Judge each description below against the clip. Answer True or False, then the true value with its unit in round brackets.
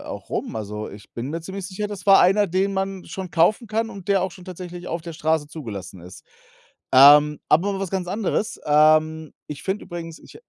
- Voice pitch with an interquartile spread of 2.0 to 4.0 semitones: False (4.4 semitones)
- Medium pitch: True (175 Hz)